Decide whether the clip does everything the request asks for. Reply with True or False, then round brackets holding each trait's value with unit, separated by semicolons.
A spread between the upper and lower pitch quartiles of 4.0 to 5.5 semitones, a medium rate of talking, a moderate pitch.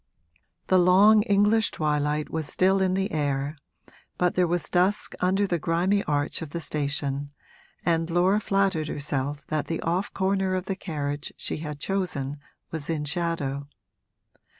True (4.3 semitones; 150 wpm; 165 Hz)